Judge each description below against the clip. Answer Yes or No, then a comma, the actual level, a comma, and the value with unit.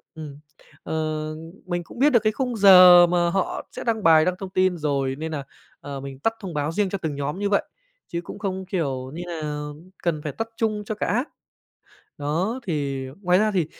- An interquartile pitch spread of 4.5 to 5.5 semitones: Yes, average, 5.1 semitones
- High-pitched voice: No, medium, 175 Hz